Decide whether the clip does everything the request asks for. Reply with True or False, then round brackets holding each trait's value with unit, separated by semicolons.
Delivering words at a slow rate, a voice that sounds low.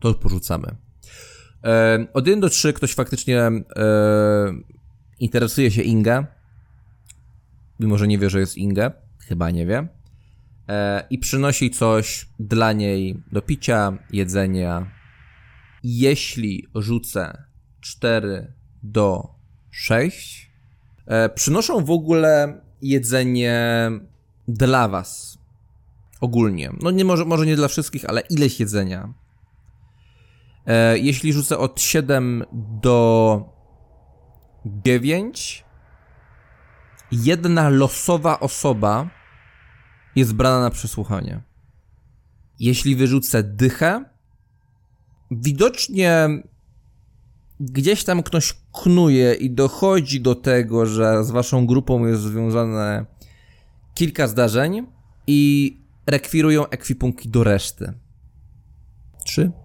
True (95 wpm; 120 Hz)